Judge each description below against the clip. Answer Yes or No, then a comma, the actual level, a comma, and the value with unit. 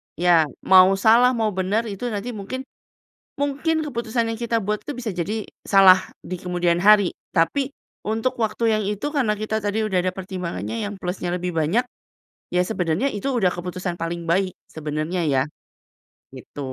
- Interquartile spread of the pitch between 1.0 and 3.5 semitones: No, average, 4.1 semitones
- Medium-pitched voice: No, high, 200 Hz